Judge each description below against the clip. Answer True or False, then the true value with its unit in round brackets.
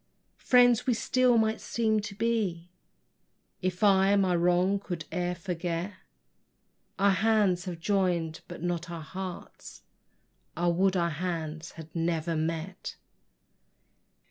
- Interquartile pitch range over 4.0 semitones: False (3.1 semitones)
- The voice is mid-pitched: True (180 Hz)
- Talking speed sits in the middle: False (120 wpm)